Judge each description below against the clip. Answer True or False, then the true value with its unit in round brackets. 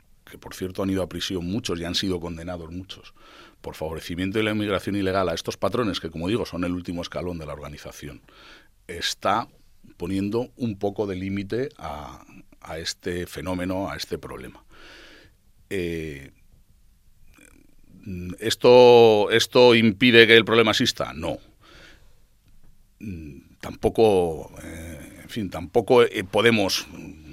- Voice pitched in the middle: False (95 Hz)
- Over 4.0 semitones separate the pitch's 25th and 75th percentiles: False (3.7 semitones)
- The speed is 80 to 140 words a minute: True (135 wpm)